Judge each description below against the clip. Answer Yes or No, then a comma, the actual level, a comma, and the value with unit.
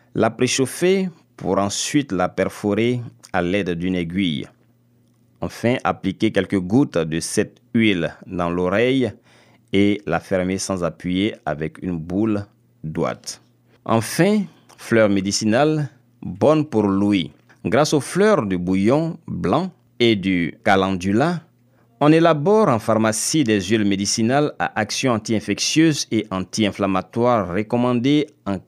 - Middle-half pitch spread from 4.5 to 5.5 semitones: Yes, average, 4.9 semitones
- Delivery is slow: Yes, slow, 120 wpm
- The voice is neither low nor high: No, low, 110 Hz